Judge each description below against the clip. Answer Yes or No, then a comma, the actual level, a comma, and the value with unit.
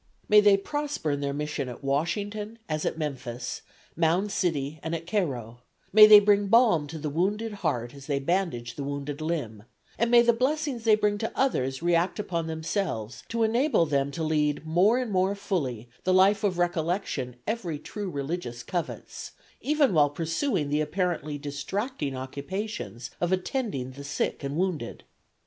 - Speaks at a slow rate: No, average, 165 wpm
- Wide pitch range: Yes, wide, 6.4 semitones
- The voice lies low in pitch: No, medium, 165 Hz